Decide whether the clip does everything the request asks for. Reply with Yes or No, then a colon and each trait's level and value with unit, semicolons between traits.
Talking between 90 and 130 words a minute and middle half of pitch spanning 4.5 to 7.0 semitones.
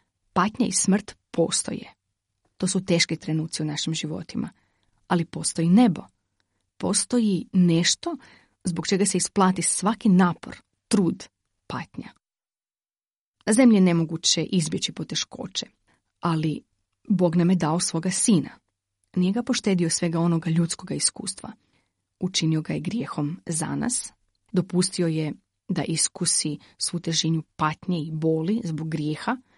No: average, 120 wpm; average, 3.2 semitones